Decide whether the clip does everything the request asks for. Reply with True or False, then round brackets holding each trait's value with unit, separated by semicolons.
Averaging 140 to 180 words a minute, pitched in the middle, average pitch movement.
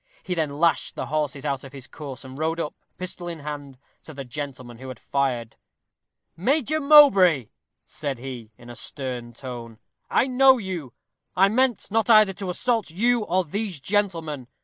False (170 wpm; 155 Hz; 7.1 semitones)